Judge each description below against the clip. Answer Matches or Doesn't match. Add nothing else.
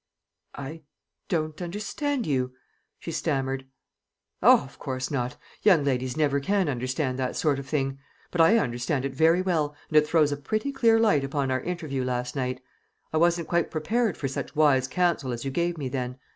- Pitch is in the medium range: Matches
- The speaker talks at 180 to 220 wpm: Matches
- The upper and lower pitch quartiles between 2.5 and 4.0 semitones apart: Doesn't match